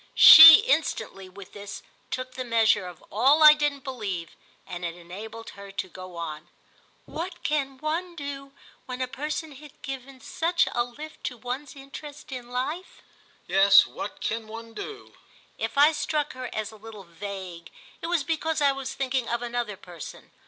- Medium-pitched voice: No, very high, 250 Hz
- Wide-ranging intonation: Yes, wide, 6.6 semitones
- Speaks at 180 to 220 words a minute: No, average, 170 wpm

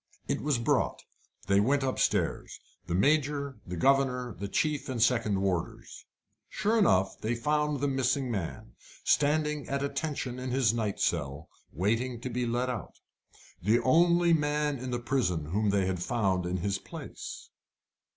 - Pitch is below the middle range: Yes, low, 125 Hz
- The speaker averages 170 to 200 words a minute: No, average, 155 wpm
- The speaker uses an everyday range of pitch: No, wide, 6.1 semitones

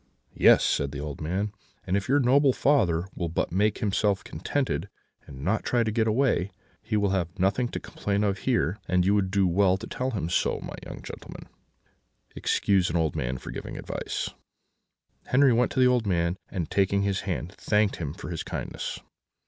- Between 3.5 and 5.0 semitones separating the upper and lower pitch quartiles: Yes, average, 3.9 semitones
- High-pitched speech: No, low, 100 Hz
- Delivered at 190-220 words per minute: Yes, average, 200 wpm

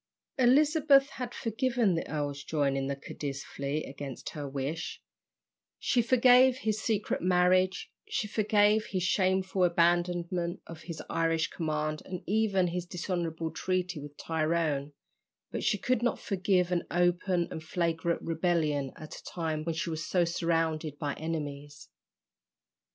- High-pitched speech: No, medium, 170 Hz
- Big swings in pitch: No, average, 3.6 semitones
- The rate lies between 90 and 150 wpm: Yes, average, 140 wpm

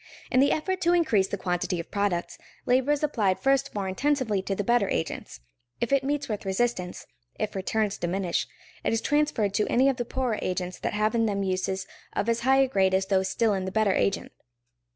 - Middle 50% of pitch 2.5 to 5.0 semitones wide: No, wide, 5.5 semitones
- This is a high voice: Yes, high, 210 Hz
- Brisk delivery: Yes, fast, 210 wpm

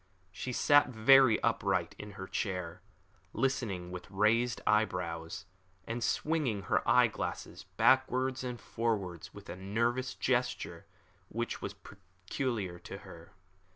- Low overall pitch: Yes, low, 105 Hz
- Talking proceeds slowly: Yes, slow, 120 wpm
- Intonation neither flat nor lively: Yes, average, 4.9 semitones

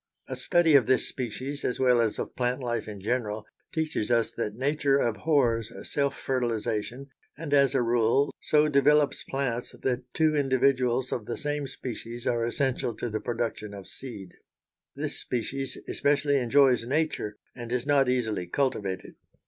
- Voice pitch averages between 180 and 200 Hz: No, low, 125 Hz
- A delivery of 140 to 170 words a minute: Yes, average, 155 wpm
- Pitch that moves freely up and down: No, average, 3.2 semitones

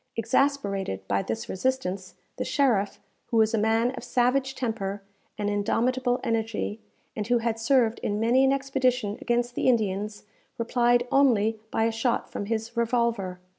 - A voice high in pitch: Yes, high, 230 Hz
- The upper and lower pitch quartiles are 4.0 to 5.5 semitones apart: No, average, 3.2 semitones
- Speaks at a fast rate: No, average, 155 wpm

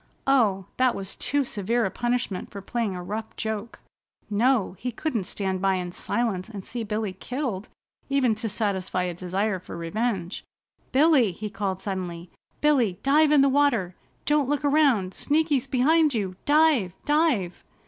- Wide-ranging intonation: Yes, wide, 6.2 semitones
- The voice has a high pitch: Yes, high, 220 Hz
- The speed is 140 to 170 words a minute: Yes, average, 160 wpm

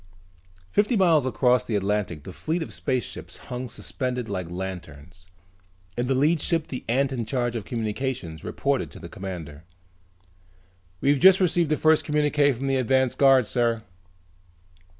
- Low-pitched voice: Yes, low, 125 Hz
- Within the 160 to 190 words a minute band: No, average, 150 wpm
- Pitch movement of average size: No, wide, 5.7 semitones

